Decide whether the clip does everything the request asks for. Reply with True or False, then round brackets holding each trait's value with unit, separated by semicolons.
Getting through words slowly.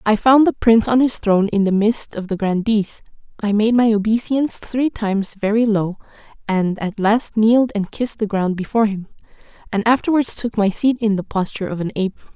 False (205 wpm)